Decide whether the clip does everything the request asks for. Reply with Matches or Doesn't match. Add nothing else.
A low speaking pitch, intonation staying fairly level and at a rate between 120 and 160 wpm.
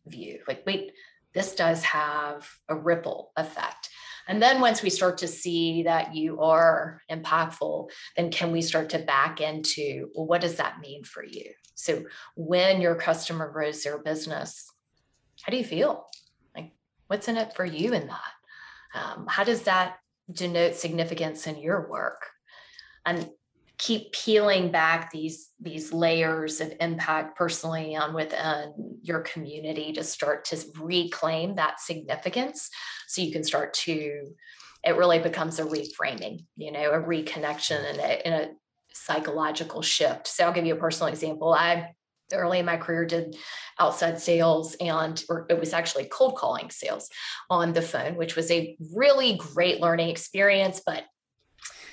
Doesn't match